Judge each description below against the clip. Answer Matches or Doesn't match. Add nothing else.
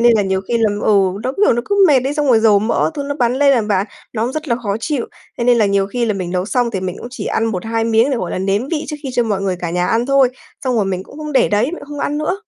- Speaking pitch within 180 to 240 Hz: Matches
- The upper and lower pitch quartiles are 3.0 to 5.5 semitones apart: Matches